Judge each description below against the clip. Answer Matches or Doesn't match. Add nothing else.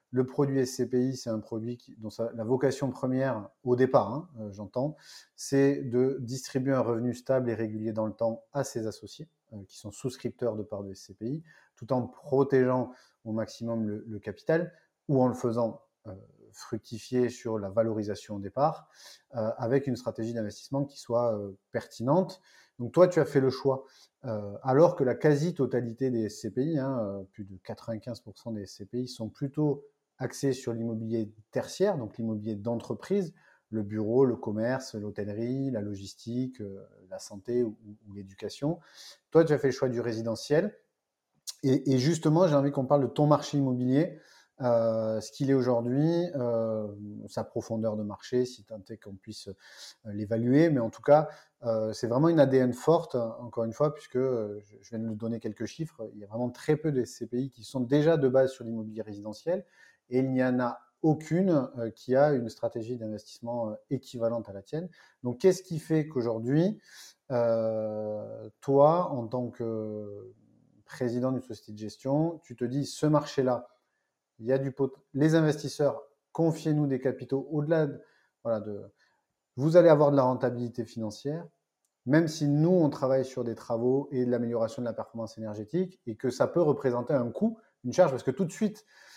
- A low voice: Matches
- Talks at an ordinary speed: Matches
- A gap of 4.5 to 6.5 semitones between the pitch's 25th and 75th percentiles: Doesn't match